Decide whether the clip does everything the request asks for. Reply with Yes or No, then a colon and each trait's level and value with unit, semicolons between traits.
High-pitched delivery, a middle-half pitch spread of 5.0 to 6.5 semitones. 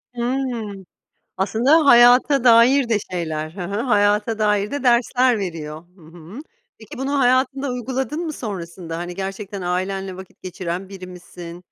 Yes: high, 205 Hz; wide, 5.5 semitones